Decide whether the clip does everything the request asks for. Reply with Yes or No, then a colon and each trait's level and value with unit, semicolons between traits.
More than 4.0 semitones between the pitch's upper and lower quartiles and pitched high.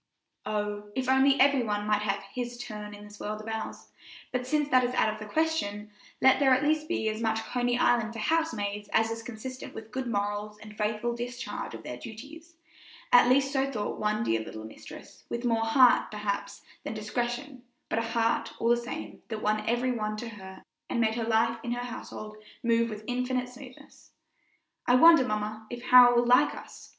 No: average, 2.9 semitones; high, 230 Hz